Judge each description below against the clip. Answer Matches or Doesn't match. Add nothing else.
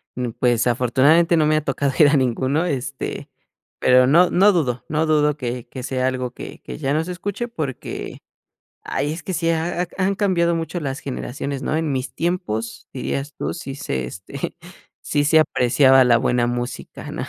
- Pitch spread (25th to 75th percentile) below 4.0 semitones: Doesn't match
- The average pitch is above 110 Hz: Matches